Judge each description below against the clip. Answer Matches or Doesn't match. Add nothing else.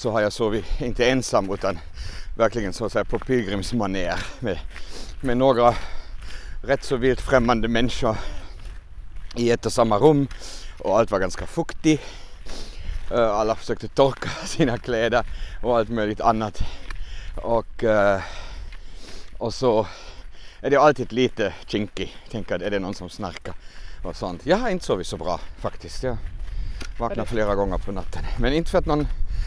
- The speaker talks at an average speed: Matches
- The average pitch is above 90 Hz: Matches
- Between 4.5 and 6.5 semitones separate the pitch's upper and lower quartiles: Matches